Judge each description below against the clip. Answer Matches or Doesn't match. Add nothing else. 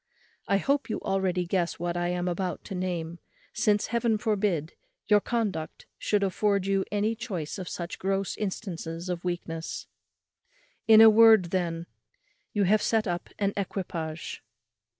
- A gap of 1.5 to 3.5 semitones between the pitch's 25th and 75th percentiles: Matches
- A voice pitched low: Doesn't match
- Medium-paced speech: Matches